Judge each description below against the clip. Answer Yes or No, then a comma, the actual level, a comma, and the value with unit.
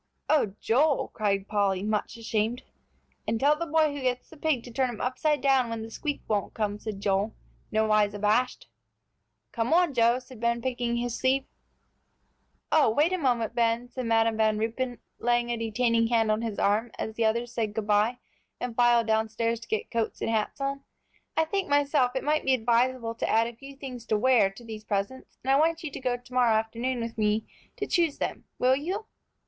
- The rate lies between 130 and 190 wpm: No, fast, 205 wpm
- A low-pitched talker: No, high, 235 Hz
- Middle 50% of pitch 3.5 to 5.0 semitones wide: No, average, 2.9 semitones